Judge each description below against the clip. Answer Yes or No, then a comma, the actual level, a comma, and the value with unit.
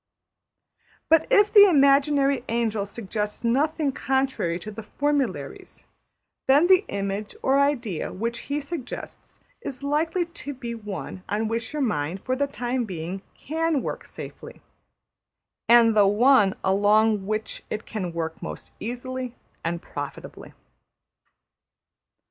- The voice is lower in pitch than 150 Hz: No, high, 235 Hz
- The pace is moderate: No, slow, 125 wpm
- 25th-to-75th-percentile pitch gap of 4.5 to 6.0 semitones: Yes, wide, 5.4 semitones